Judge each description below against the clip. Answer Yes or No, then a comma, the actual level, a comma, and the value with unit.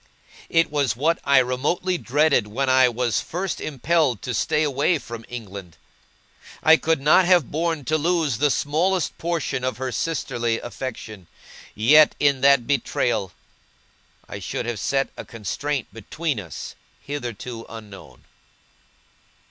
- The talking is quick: No, slow, 135 wpm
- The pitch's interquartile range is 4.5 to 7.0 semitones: Yes, average, 4.8 semitones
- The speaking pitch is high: No, low, 135 Hz